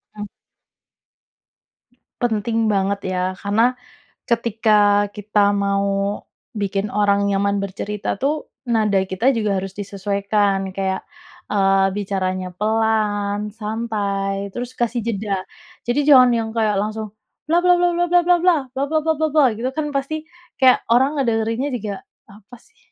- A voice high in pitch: Yes, high, 210 Hz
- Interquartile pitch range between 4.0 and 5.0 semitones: No, average, 3.3 semitones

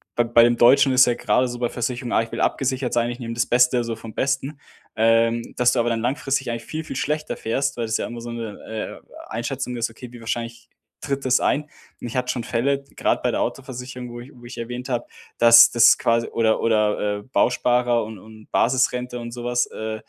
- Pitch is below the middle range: Yes, low, 120 Hz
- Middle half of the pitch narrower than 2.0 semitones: Yes, narrow, 1.5 semitones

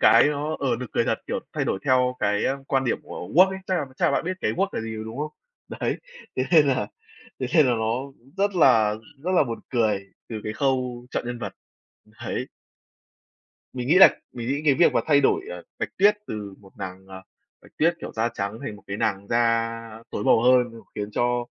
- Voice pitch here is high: No, low, 120 Hz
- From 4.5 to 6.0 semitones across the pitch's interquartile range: Yes, average, 4.8 semitones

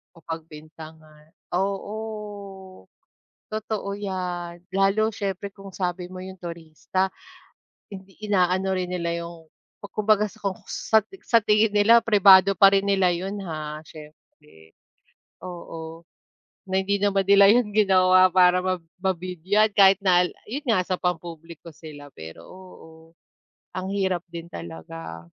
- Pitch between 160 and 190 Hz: Yes, medium, 185 Hz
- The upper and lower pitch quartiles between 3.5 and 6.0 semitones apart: No, average, 2.9 semitones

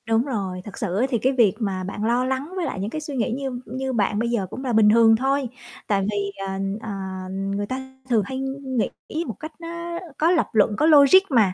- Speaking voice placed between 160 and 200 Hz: No, high, 240 Hz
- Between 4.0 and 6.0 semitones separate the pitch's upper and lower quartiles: Yes, average, 4.8 semitones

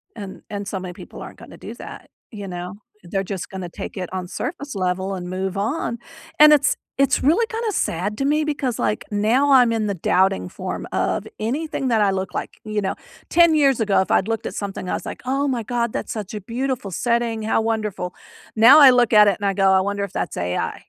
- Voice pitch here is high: Yes, high, 215 Hz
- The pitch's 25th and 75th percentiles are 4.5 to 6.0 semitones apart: Yes, average, 5.1 semitones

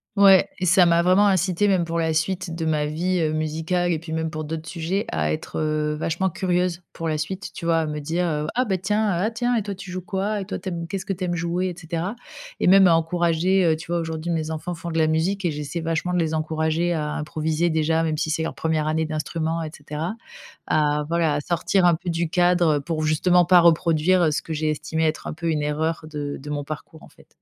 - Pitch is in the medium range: Yes, medium, 165 Hz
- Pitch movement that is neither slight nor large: No, narrow, 2.3 semitones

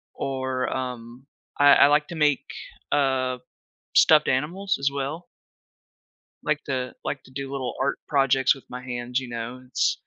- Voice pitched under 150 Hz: Yes, low, 135 Hz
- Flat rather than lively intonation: Yes, narrow, 2.1 semitones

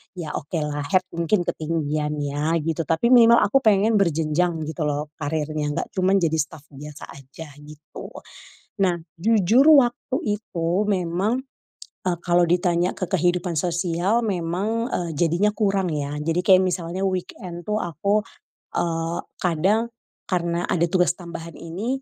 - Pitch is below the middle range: No, medium, 175 Hz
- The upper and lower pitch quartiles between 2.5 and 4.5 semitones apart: Yes, average, 3.4 semitones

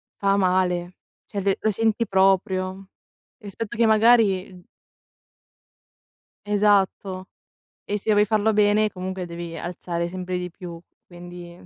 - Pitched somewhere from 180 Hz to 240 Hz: Yes, high, 190 Hz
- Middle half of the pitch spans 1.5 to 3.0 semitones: Yes, narrow, 2.5 semitones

